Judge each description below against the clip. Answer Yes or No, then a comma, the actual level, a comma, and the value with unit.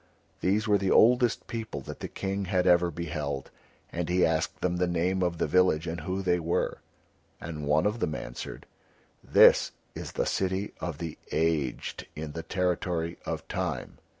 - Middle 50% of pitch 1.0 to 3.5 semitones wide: Yes, narrow, 2.5 semitones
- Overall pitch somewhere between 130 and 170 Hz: No, very low, 90 Hz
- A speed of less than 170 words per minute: No, average, 175 wpm